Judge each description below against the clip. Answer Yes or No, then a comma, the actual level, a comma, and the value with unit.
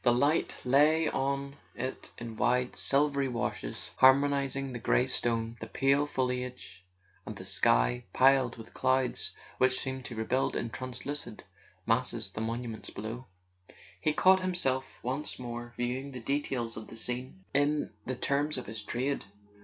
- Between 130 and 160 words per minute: Yes, average, 150 wpm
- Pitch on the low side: Yes, low, 130 Hz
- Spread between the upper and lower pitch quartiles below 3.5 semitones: Yes, average, 2.8 semitones